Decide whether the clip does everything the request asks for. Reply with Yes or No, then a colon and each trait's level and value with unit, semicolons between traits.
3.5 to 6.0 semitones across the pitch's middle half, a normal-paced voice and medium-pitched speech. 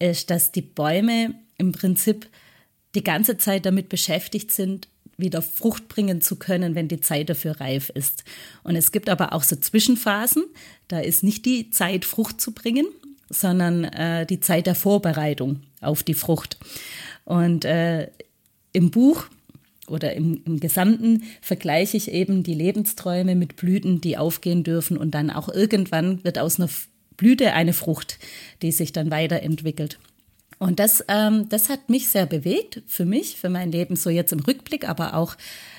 Yes: average, 4.2 semitones; average, 165 wpm; medium, 180 Hz